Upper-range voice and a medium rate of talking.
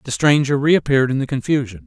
No: low, 130 Hz; average, 195 wpm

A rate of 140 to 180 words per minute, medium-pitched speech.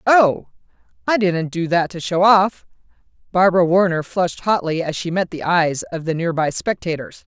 Yes: average, 170 wpm; medium, 175 Hz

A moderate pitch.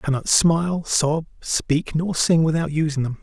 Yes: medium, 155 Hz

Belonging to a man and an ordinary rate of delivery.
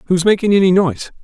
Yes: male; average, 195 wpm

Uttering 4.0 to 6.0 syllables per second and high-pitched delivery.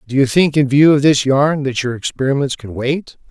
No: 5.2 syllables/s; medium, 140 Hz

